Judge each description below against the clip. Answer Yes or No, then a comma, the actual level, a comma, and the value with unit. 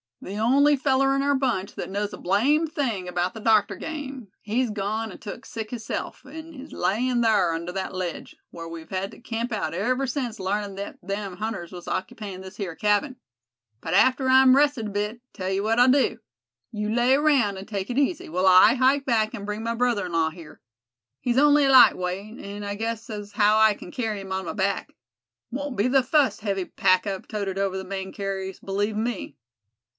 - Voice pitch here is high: Yes, high, 210 Hz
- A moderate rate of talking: No, fast, 210 wpm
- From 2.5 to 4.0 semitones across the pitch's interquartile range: No, average, 4.7 semitones